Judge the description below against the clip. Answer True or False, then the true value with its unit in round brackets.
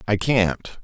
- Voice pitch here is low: True (105 Hz)